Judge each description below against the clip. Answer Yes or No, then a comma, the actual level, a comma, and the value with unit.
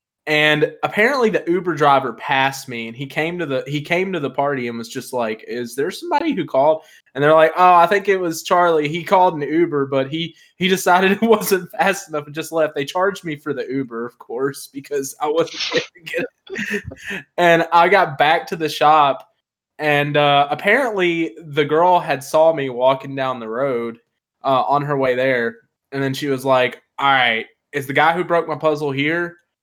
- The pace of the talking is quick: Yes, fast, 210 wpm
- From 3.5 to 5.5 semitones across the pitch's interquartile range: Yes, average, 4.1 semitones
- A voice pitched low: No, medium, 155 Hz